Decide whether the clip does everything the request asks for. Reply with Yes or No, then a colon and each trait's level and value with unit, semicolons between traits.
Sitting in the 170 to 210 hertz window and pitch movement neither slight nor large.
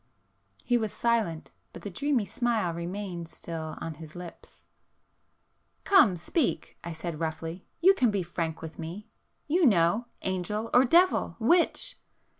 No: high, 190 Hz; wide, 6.3 semitones